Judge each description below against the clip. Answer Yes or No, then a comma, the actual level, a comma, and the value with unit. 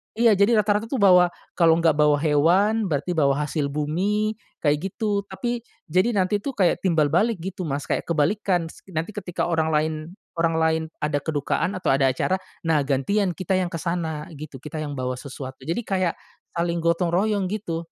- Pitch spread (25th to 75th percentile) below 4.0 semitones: No, average, 4.5 semitones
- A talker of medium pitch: Yes, medium, 170 Hz